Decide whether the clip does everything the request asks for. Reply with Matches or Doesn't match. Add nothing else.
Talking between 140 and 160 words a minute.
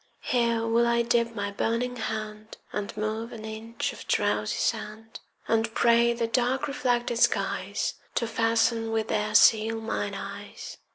Matches